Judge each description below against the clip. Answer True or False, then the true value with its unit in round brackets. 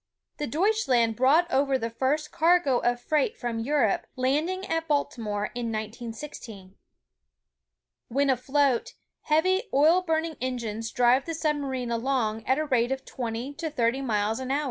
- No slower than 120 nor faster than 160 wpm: True (150 wpm)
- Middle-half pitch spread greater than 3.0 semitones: True (4.5 semitones)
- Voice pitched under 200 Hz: False (265 Hz)